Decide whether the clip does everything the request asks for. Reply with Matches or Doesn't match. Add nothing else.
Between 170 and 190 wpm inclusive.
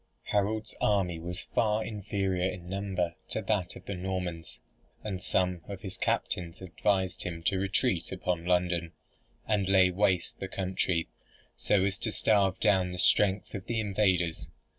Doesn't match